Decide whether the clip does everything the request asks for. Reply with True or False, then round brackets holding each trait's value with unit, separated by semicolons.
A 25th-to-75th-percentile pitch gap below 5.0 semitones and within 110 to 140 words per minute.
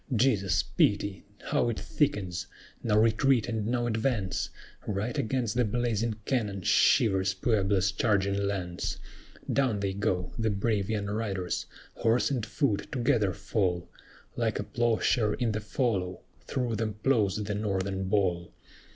True (3.1 semitones; 135 wpm)